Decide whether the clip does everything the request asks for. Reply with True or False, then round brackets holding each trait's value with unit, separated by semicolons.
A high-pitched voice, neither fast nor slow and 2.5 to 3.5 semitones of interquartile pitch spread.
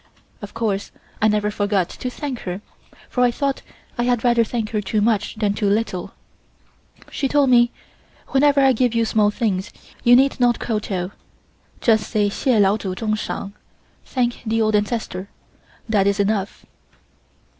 True (220 Hz; 165 wpm; 2.9 semitones)